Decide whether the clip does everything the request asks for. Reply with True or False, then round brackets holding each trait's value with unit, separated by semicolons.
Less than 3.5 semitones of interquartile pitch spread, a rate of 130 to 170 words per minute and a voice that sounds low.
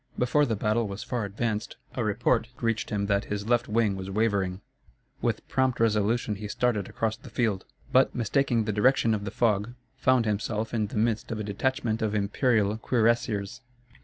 False (2.4 semitones; 180 wpm; 110 Hz)